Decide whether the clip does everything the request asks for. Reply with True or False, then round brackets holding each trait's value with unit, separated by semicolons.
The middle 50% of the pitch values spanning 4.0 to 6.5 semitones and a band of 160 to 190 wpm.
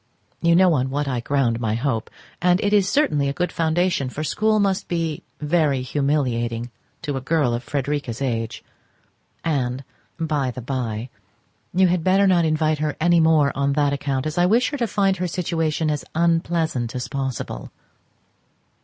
True (4.6 semitones; 170 wpm)